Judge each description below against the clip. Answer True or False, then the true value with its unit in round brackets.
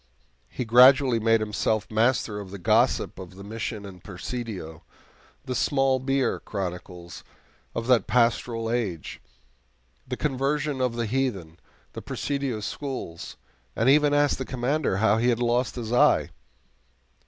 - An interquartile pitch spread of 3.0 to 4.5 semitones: True (4.2 semitones)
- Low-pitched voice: True (120 Hz)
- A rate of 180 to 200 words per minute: False (140 wpm)